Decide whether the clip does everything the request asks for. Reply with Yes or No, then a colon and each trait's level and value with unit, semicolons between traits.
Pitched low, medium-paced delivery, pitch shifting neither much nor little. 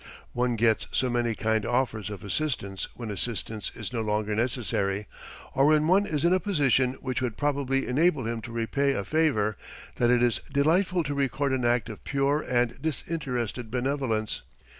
Yes: low, 125 Hz; average, 175 wpm; average, 4.0 semitones